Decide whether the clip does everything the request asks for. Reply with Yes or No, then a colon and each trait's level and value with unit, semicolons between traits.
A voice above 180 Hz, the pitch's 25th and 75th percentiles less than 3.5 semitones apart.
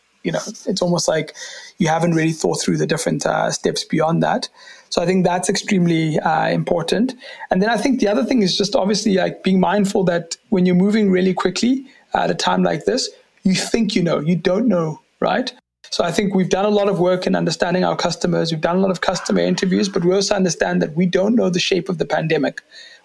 Yes: high, 190 Hz; average, 2.7 semitones